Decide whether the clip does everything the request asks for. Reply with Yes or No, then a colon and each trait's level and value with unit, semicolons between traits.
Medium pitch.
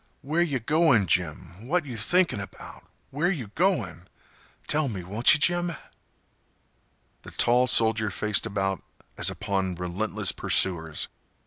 No: low, 110 Hz